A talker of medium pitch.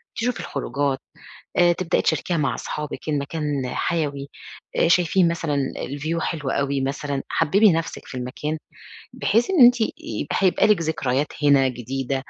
Yes: medium, 150 Hz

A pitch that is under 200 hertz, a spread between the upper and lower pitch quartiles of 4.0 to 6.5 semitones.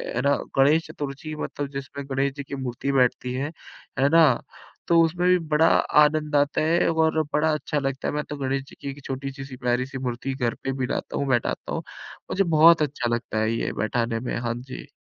No: medium, 140 Hz; average, 2.9 semitones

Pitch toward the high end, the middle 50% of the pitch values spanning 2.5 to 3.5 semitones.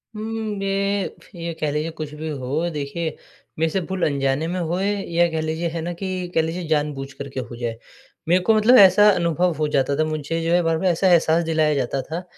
No: medium, 165 Hz; average, 3.2 semitones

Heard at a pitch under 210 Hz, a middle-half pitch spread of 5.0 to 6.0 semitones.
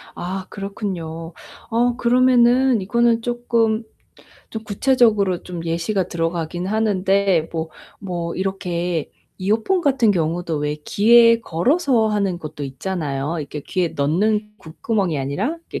Yes: high, 195 Hz; wide, 5.4 semitones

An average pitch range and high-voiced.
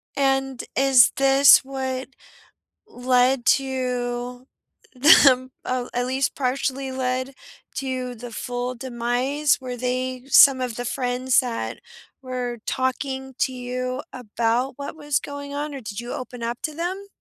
No: narrow, 1.5 semitones; very high, 255 Hz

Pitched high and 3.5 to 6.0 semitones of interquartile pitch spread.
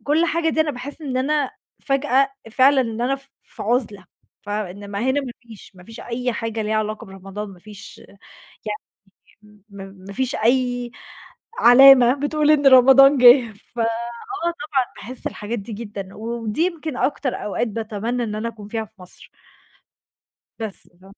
Yes: high, 235 Hz; average, 4.3 semitones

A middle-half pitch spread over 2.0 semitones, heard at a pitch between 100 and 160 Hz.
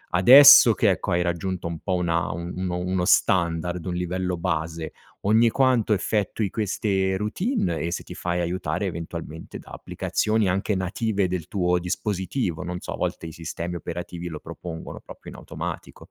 No: narrow, 2.6 semitones; very low, 90 Hz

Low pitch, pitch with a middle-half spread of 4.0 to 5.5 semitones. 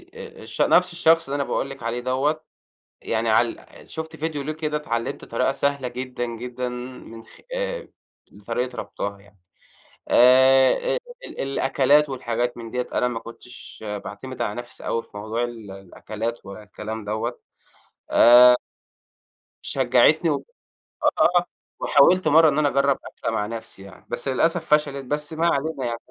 Yes: low, 125 Hz; average, 4.3 semitones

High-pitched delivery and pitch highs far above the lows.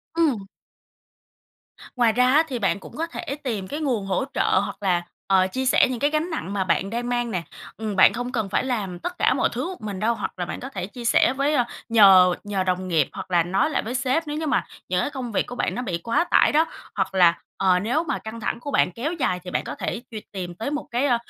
Yes: high, 230 Hz; wide, 5.8 semitones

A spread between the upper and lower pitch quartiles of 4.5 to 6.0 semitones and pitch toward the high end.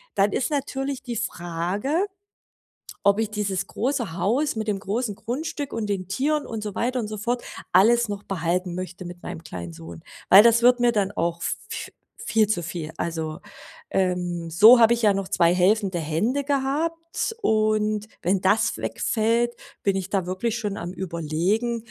Yes: average, 4.8 semitones; high, 205 Hz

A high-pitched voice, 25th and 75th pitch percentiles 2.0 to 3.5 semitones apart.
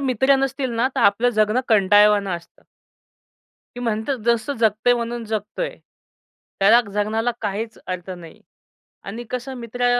Yes: high, 225 Hz; average, 3.0 semitones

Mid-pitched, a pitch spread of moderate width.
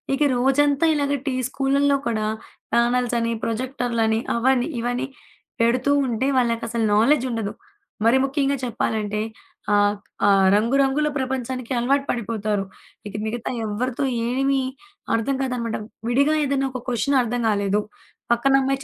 No: high, 245 Hz; average, 3.1 semitones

